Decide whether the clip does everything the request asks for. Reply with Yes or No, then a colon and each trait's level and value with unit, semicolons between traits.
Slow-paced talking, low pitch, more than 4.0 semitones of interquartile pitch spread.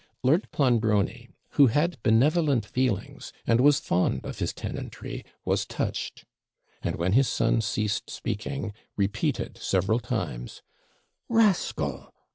Yes: slow, 115 wpm; low, 115 Hz; average, 5.1 semitones